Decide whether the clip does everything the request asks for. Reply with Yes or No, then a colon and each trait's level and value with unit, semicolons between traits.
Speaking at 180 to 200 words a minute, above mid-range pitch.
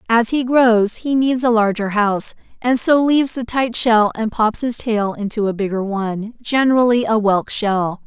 Yes: average, 195 wpm; high, 225 Hz